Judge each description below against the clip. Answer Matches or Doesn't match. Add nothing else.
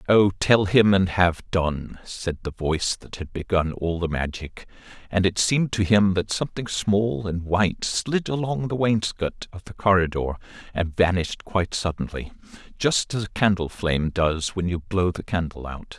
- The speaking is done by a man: Matches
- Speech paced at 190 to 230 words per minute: Doesn't match